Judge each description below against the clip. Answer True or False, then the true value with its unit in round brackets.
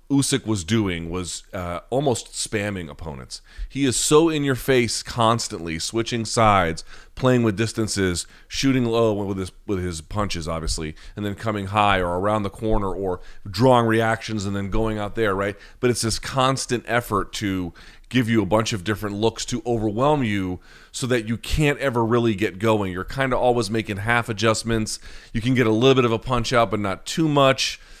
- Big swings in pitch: False (3.4 semitones)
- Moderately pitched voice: False (110 Hz)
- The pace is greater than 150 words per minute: True (195 wpm)